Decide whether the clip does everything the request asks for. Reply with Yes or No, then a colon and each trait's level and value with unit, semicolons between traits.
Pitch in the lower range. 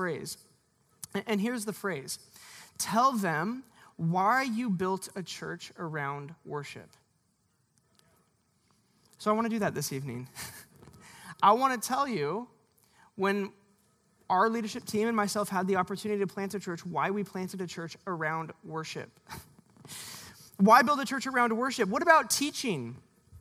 No: high, 200 Hz